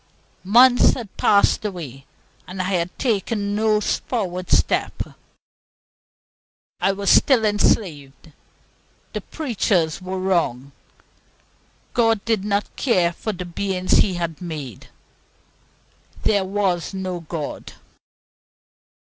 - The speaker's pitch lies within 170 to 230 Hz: Yes, high, 190 Hz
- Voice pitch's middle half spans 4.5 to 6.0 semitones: No, average, 3.4 semitones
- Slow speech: Yes, slow, 105 wpm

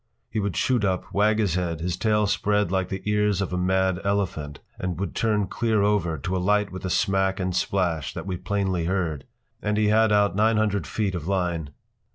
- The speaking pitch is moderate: No, very low, 95 Hz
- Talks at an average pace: No, fast, 210 wpm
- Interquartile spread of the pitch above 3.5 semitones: No, narrow, 2.4 semitones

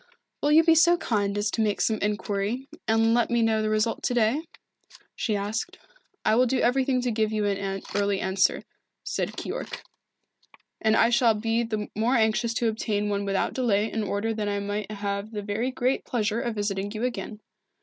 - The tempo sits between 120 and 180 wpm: No, average, 195 wpm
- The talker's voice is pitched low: No, high, 220 Hz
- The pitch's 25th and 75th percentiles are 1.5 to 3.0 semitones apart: Yes, narrow, 2.4 semitones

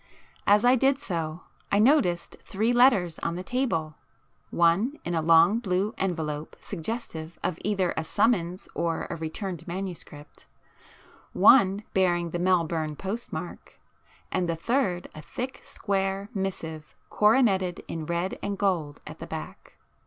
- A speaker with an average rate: No, slow, 130 wpm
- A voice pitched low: No, medium, 185 Hz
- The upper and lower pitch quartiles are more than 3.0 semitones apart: Yes, average, 3.9 semitones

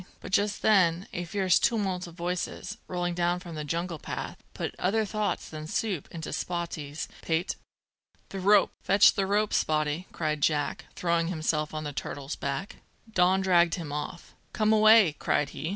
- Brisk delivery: No, average, 170 wpm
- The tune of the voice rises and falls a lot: No, average, 3.7 semitones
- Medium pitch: Yes, medium, 175 Hz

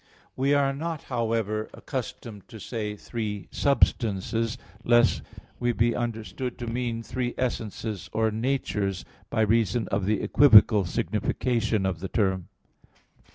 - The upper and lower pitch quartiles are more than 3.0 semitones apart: No, narrow, 2.6 semitones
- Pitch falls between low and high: No, low, 115 Hz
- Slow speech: Yes, slow, 125 wpm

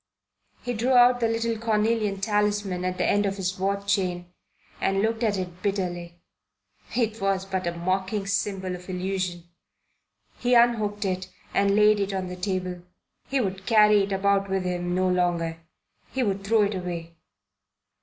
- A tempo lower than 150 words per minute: No, average, 165 wpm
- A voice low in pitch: No, high, 195 Hz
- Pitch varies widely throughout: No, narrow, 2.5 semitones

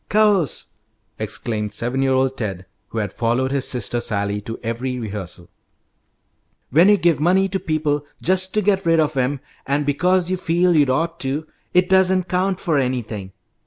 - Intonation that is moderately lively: No, wide, 7.0 semitones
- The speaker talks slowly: No, average, 170 wpm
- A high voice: No, medium, 145 Hz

